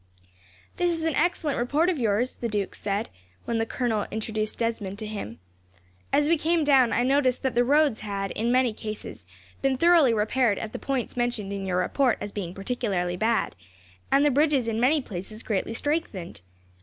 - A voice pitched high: Yes, high, 235 Hz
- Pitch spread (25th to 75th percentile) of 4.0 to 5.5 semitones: Yes, average, 4.9 semitones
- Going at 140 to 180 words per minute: No, average, 190 wpm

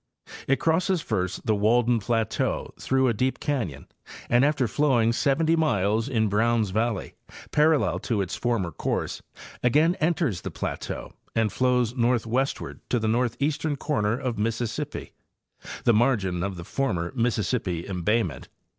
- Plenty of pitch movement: No, average, 4.2 semitones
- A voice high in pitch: No, low, 120 Hz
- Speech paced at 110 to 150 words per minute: Yes, average, 140 wpm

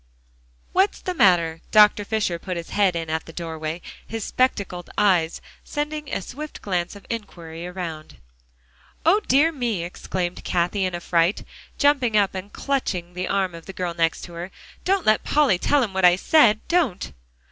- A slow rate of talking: No, average, 175 wpm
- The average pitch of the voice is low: No, high, 190 Hz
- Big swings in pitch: Yes, wide, 5.7 semitones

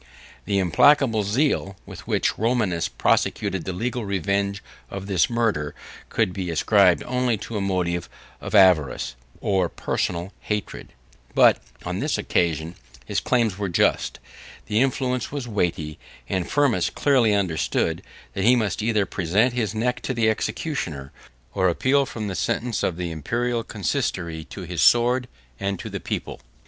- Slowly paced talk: No, average, 150 wpm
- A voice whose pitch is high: No, low, 100 Hz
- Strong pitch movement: No, average, 5.0 semitones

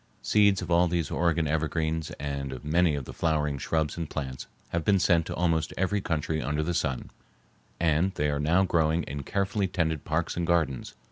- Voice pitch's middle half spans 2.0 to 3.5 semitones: Yes, narrow, 2.6 semitones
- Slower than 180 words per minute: No, average, 195 wpm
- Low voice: Yes, very low, 80 Hz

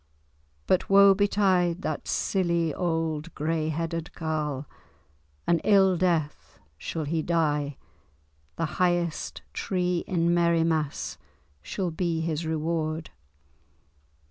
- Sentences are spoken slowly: Yes, slow, 100 wpm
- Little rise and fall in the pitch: Yes, narrow, 2.0 semitones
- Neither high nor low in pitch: Yes, medium, 165 Hz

